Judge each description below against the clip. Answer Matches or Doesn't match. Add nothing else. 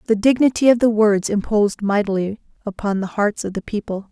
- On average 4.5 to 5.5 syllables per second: Doesn't match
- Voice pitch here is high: Matches